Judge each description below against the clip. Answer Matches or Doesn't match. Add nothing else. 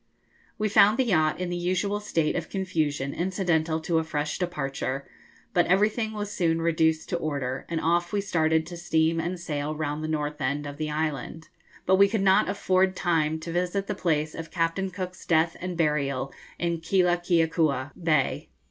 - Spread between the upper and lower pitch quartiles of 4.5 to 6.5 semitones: Doesn't match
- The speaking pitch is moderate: Matches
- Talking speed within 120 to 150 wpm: Doesn't match